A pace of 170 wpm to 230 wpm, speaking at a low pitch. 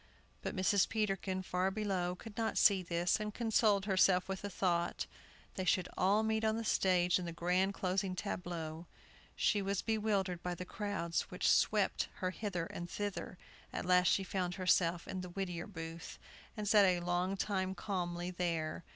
No: average, 175 wpm; medium, 185 Hz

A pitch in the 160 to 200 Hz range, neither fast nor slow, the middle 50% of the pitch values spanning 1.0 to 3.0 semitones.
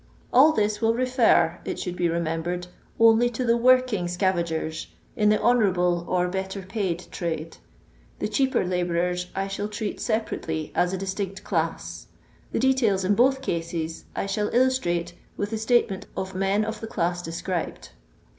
No: high, 190 Hz; average, 165 wpm; average, 4.3 semitones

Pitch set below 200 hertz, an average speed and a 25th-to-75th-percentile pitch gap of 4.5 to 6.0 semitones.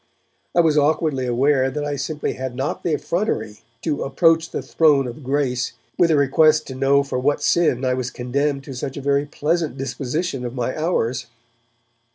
No: medium, 140 Hz; average, 185 wpm; average, 3.0 semitones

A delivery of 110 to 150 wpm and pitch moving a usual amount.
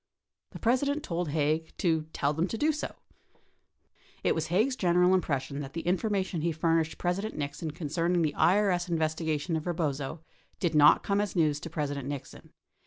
No: average, 175 wpm; average, 3.2 semitones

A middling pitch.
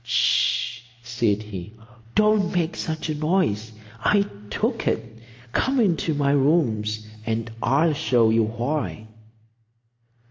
No: low, 130 Hz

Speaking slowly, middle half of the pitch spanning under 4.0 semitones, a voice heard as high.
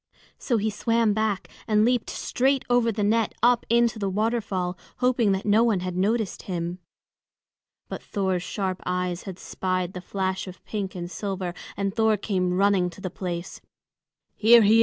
No: average, 175 wpm; average, 3.4 semitones; high, 200 Hz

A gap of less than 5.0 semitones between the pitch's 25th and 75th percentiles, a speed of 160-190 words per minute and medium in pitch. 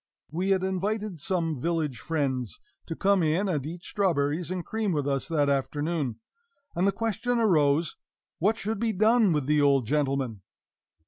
No: wide, 5.4 semitones; average, 165 wpm; medium, 165 Hz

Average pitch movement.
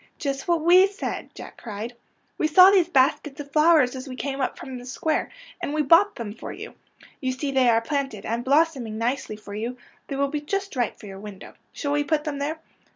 Yes: average, 4.2 semitones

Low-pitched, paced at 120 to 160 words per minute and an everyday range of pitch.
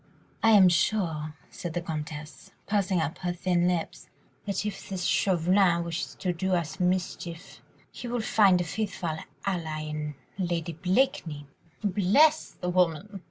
No: medium, 180 Hz; average, 145 wpm; average, 3.0 semitones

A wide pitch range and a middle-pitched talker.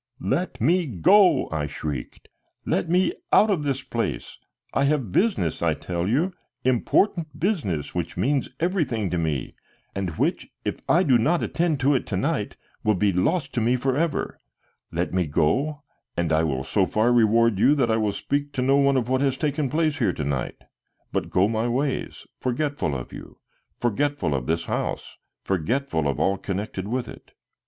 No: wide, 8.0 semitones; low, 120 Hz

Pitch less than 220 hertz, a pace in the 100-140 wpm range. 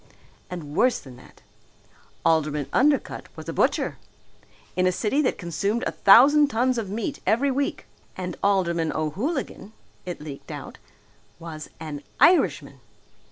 Yes: high, 190 Hz; slow, 135 wpm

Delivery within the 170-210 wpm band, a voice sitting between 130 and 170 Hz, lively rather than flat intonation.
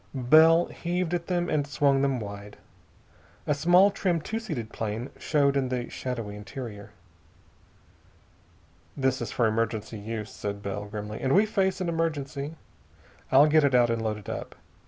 No: average, 160 wpm; low, 135 Hz; wide, 6.7 semitones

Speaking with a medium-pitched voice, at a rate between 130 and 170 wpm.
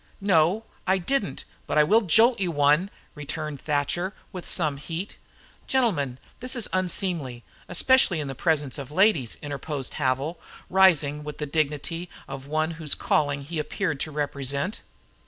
Yes: medium, 155 Hz; average, 150 wpm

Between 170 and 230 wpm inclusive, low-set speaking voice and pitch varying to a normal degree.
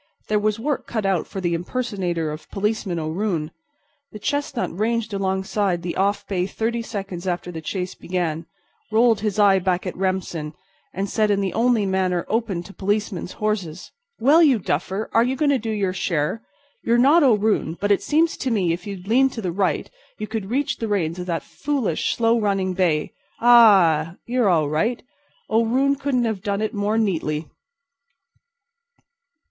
No: average, 175 wpm; high, 200 Hz; average, 4.1 semitones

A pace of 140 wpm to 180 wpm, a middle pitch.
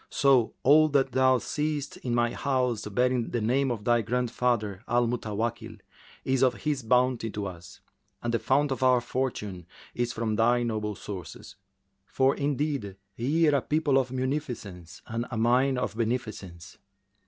No: average, 155 wpm; low, 120 Hz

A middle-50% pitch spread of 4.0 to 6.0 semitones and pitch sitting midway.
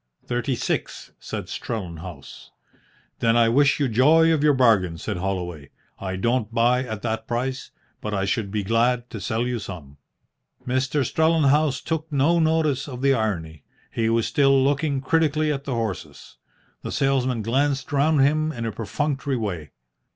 No: average, 4.9 semitones; low, 125 Hz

